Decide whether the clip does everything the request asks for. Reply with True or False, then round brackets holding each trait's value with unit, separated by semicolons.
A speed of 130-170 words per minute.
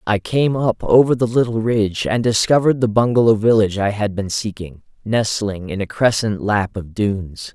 False (185 wpm)